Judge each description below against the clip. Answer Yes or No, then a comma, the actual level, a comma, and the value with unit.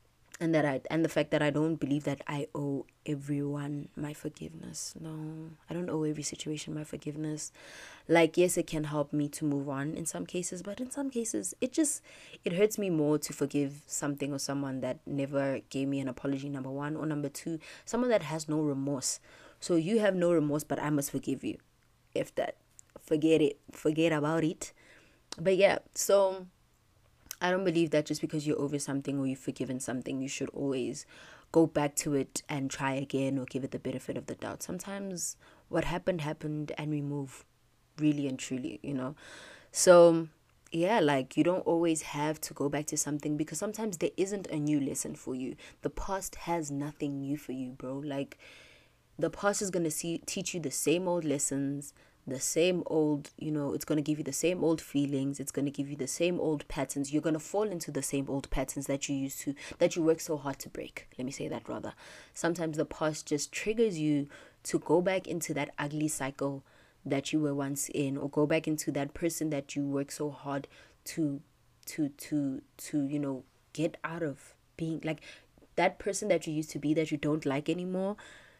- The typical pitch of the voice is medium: Yes, medium, 150 Hz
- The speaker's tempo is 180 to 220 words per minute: Yes, fast, 205 wpm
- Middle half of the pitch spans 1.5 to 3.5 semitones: Yes, average, 2.7 semitones